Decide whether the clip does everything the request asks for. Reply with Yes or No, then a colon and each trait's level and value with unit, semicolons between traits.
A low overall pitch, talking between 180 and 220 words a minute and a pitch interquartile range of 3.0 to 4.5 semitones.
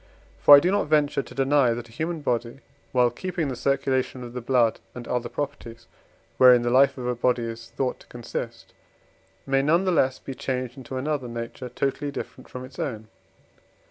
No: low, 130 Hz; average, 195 wpm; narrow, 2.5 semitones